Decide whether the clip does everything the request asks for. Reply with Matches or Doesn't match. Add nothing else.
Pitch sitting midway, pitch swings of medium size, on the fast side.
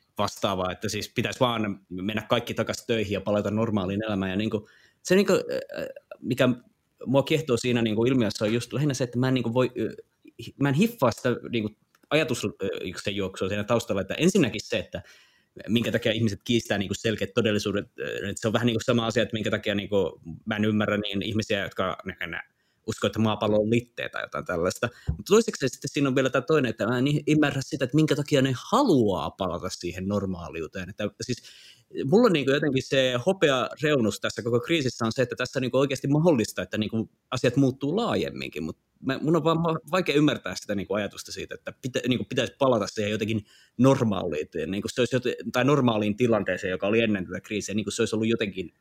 Doesn't match